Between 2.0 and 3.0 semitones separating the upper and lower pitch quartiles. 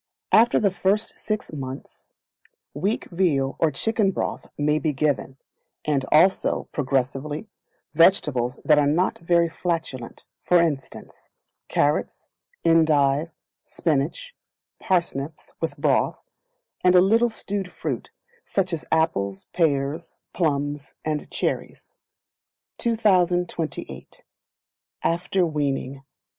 No: average, 4.3 semitones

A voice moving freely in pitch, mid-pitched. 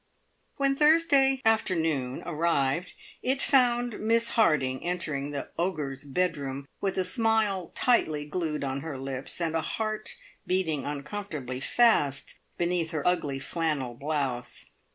Yes: wide, 7.4 semitones; medium, 165 Hz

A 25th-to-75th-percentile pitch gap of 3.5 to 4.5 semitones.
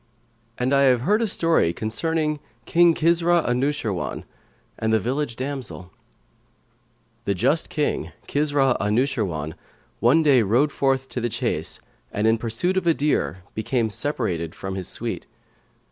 No: wide, 5.5 semitones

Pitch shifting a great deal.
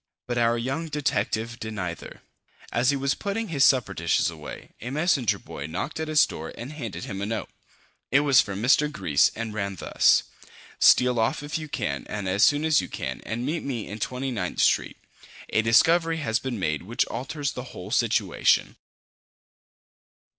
Yes: wide, 5.7 semitones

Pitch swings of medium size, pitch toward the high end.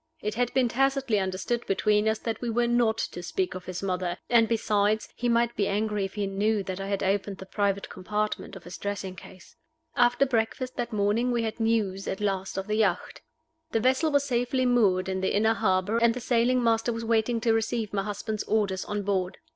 Yes: average, 3.2 semitones; high, 215 Hz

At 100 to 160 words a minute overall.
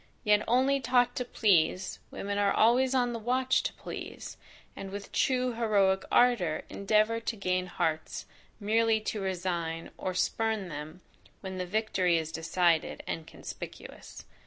Yes: average, 145 wpm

